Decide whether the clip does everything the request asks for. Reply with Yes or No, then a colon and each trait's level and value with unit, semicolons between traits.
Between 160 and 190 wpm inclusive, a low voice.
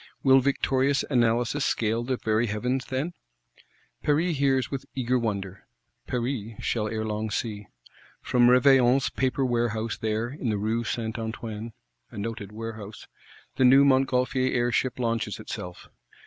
No: slow, 135 wpm; low, 120 Hz